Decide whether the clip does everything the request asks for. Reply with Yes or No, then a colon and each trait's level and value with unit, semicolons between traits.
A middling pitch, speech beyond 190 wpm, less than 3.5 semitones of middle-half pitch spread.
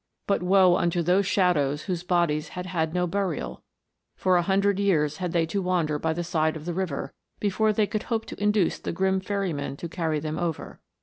Yes: medium, 180 Hz; fast, 205 wpm; average, 3.1 semitones